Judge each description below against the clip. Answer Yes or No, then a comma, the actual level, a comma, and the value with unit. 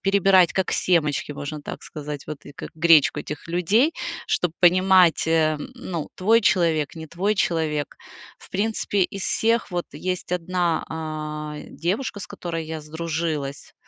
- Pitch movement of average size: Yes, average, 3.3 semitones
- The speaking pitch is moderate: Yes, medium, 165 Hz